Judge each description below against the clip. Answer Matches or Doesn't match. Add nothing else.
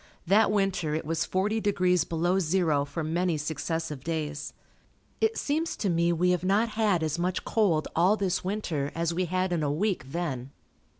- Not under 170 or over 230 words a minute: Matches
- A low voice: Doesn't match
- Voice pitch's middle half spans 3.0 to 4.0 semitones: Matches